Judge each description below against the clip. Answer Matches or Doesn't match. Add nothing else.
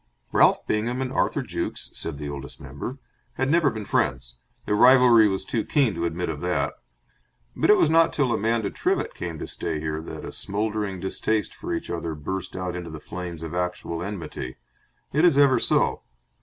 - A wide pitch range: Matches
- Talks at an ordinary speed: Matches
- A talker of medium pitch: Doesn't match